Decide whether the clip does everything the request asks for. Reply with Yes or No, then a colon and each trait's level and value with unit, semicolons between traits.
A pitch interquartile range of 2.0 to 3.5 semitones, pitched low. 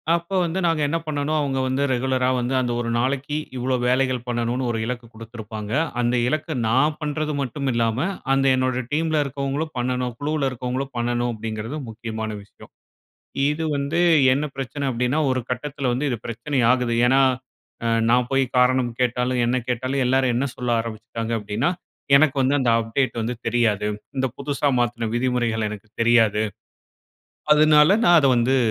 Yes: average, 3.0 semitones; low, 125 Hz